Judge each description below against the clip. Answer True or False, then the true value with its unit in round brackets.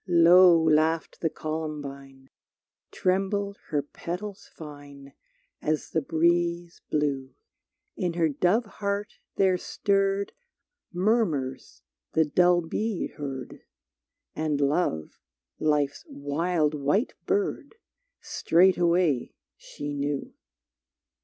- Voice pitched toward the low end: False (160 Hz)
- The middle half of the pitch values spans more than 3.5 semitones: True (4.1 semitones)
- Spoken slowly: True (90 wpm)